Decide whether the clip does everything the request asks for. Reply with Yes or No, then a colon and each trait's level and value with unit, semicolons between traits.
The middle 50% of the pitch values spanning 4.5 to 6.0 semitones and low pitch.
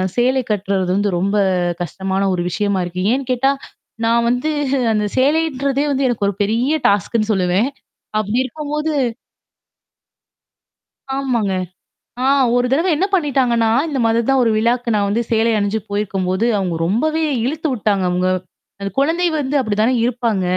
No: average, 5.0 semitones; high, 230 Hz